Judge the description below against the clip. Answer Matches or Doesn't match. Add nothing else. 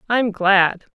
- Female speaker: Matches